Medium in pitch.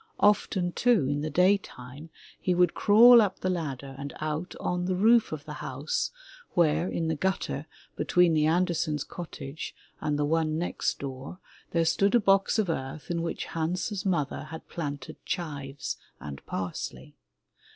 Yes: medium, 165 Hz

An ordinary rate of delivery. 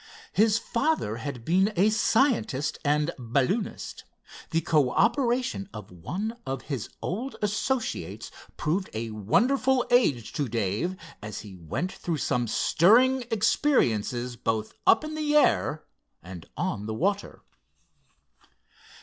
No: slow, 120 wpm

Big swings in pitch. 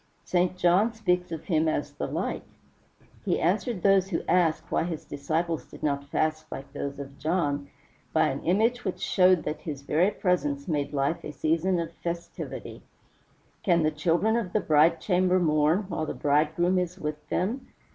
No: average, 3.2 semitones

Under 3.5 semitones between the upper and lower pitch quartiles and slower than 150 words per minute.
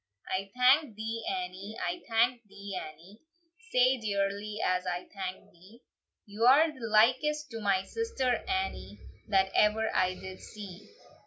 No: average, 4.7 semitones; average, 140 wpm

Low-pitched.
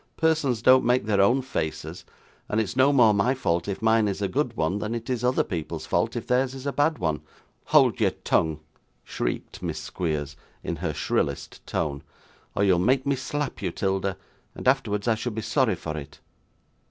Yes: low, 110 Hz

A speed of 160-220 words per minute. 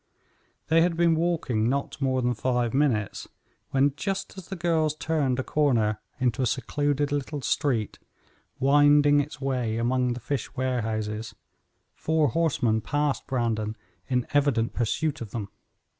No: average, 145 wpm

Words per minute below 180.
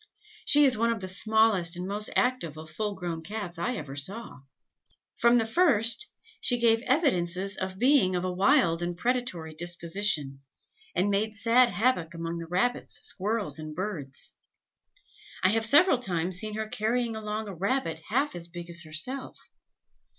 Yes: average, 165 wpm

